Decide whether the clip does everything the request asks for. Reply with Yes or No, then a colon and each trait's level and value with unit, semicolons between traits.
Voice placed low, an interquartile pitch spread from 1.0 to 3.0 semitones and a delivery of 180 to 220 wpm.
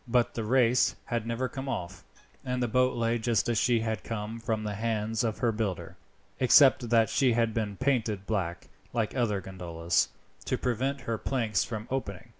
Yes: low, 115 Hz; narrow, 2.6 semitones; average, 185 wpm